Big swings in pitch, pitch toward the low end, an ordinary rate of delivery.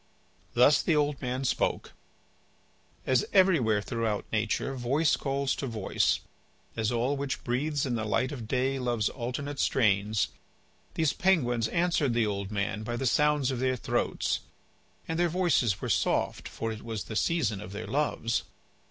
No: average, 4.5 semitones; low, 125 Hz; average, 160 wpm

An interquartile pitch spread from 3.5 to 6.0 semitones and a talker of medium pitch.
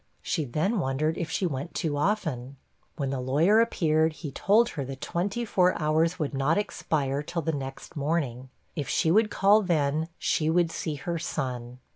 Yes: average, 4.0 semitones; medium, 155 Hz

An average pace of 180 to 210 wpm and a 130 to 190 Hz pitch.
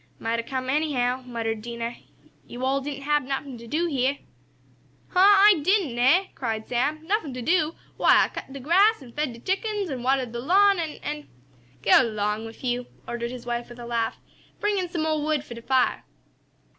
No: fast, 205 wpm; very high, 265 Hz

